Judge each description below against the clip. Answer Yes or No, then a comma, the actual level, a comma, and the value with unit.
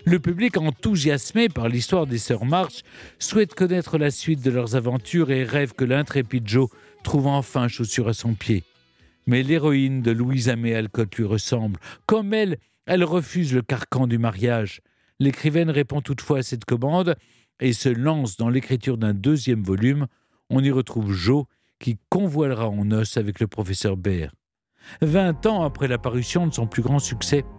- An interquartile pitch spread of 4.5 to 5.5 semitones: Yes, average, 4.8 semitones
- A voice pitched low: Yes, low, 130 Hz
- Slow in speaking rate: No, average, 165 wpm